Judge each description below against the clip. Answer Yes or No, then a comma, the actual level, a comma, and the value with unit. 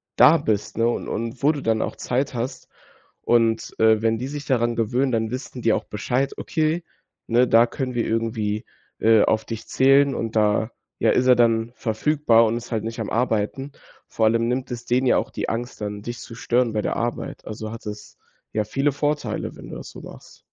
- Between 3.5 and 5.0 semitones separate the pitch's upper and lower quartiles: No, narrow, 2.4 semitones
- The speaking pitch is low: Yes, low, 115 Hz